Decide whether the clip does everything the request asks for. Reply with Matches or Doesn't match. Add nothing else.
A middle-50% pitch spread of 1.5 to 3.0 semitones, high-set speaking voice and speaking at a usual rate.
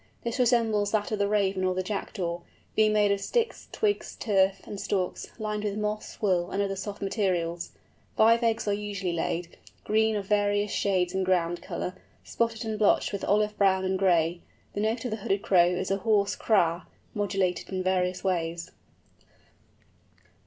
Matches